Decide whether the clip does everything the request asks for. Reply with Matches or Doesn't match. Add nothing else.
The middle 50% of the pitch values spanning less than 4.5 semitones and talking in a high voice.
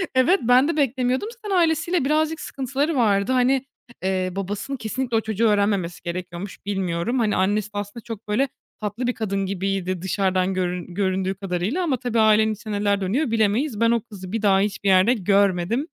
Doesn't match